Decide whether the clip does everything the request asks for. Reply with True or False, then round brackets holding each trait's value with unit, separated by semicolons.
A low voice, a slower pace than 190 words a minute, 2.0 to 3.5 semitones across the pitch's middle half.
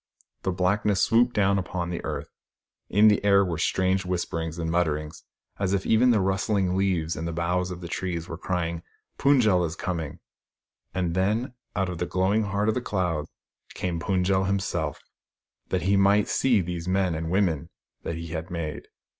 False (90 Hz; 195 wpm; 2.8 semitones)